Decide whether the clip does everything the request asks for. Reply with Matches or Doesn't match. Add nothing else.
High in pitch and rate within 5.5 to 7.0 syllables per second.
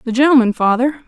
Matches